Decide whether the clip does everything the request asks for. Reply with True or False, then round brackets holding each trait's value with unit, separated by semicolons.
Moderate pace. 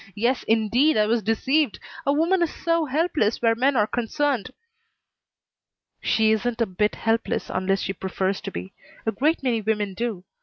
True (165 wpm)